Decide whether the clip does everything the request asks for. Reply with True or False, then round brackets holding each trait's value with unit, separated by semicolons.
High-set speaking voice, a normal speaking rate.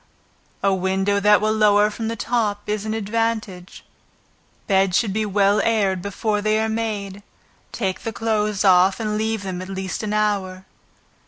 True (205 Hz; 165 wpm)